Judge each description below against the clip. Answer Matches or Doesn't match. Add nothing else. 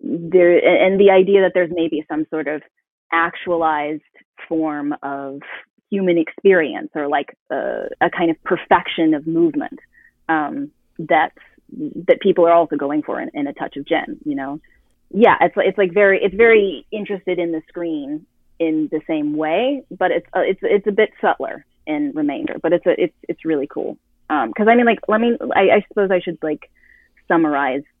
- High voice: Matches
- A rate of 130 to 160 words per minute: Doesn't match